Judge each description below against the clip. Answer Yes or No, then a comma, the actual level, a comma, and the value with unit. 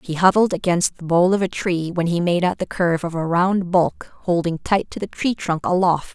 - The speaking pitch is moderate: Yes, medium, 175 Hz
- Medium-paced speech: No, fast, 245 wpm